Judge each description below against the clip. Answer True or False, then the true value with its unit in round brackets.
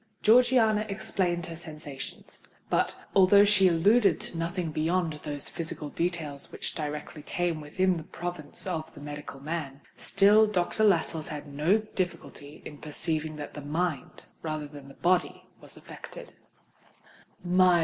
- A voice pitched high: False (165 Hz)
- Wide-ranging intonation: False (3.7 semitones)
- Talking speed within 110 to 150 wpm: True (140 wpm)